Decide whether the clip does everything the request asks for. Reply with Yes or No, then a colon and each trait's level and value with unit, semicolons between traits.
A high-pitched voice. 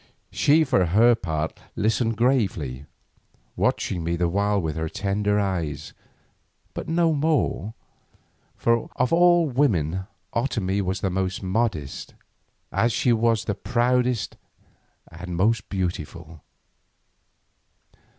No: low, 100 Hz